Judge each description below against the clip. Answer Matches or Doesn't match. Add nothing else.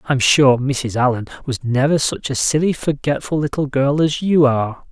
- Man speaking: Matches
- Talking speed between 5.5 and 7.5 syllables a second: Doesn't match